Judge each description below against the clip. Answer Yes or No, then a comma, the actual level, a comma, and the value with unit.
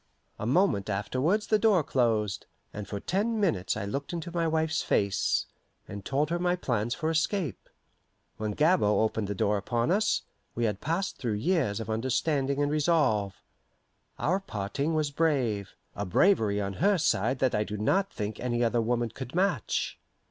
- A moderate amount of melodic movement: No, wide, 7.8 semitones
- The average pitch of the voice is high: No, low, 130 Hz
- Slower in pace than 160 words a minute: No, average, 170 wpm